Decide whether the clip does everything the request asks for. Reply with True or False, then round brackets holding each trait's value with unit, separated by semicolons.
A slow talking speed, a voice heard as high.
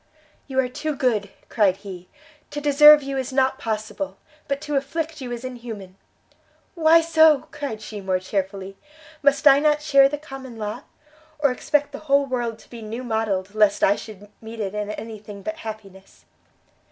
False (175 wpm; 245 Hz)